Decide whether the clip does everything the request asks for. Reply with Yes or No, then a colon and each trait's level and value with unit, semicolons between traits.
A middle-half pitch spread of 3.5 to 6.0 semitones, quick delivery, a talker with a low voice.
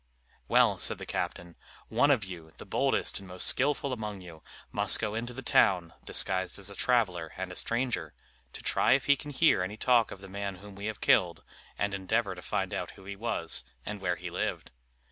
Yes: average, 4.1 semitones; fast, 210 wpm; low, 100 Hz